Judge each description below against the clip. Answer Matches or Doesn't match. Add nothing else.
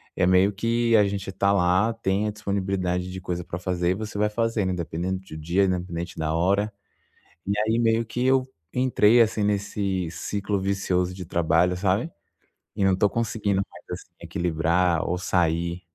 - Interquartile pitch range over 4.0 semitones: Doesn't match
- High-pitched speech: Doesn't match